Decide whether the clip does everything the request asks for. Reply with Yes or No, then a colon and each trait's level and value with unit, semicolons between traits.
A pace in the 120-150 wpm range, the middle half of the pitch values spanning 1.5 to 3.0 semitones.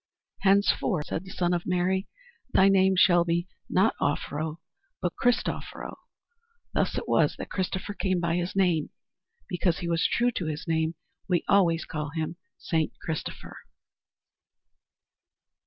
Yes: average, 140 wpm; narrow, 2.5 semitones